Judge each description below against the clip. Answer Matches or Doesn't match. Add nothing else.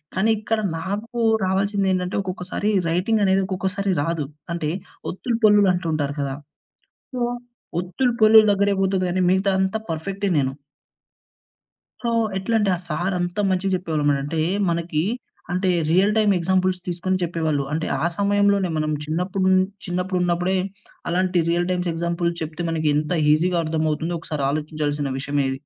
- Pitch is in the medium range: Matches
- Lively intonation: Doesn't match